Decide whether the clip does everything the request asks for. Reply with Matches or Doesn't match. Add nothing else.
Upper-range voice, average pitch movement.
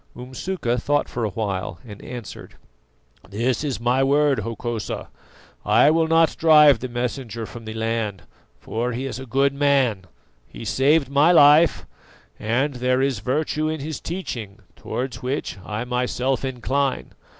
Doesn't match